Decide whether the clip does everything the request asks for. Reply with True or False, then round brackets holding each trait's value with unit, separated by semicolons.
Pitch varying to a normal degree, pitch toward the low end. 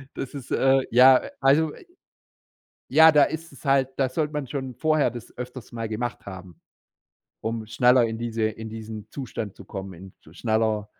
True (3.7 semitones; 120 Hz)